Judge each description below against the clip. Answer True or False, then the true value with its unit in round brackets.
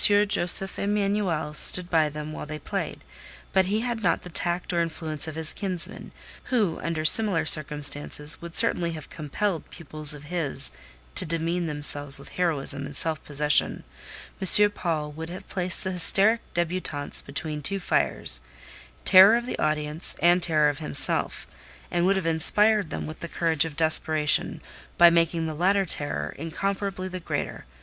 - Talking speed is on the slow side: False (160 wpm)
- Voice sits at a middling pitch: True (165 Hz)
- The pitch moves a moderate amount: True (3.5 semitones)